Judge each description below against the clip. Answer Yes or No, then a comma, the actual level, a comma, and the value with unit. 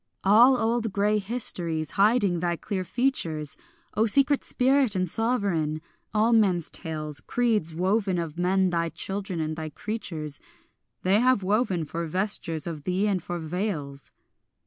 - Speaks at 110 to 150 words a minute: Yes, average, 145 wpm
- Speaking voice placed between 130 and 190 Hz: Yes, medium, 185 Hz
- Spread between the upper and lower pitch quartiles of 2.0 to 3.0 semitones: No, average, 4.8 semitones